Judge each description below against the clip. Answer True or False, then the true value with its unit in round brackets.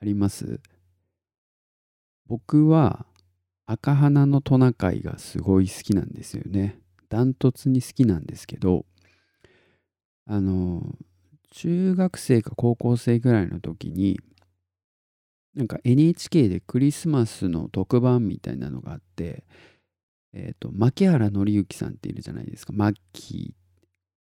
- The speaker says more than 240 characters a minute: True (250 characters per minute)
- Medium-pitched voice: False (105 Hz)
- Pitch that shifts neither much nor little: False (6.0 semitones)